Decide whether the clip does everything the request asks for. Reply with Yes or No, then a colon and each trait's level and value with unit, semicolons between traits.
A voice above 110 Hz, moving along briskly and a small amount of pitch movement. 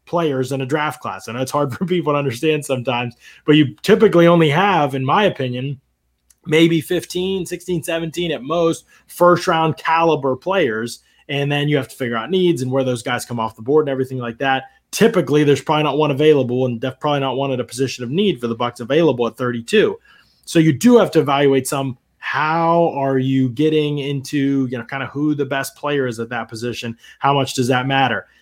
No: medium, 140 Hz; fast, 215 wpm; average, 3.9 semitones